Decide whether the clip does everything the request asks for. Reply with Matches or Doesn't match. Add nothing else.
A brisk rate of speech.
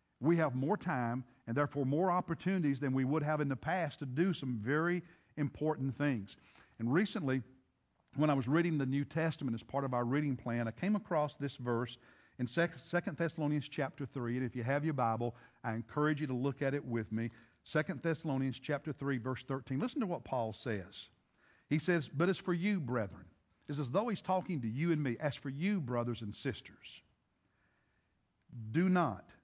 Doesn't match